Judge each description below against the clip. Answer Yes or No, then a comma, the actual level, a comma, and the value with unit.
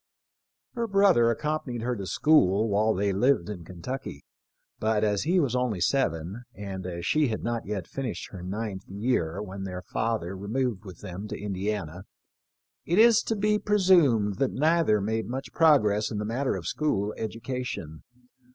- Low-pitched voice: Yes, low, 110 Hz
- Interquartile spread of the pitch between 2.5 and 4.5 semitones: No, wide, 5.6 semitones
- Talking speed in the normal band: Yes, average, 165 wpm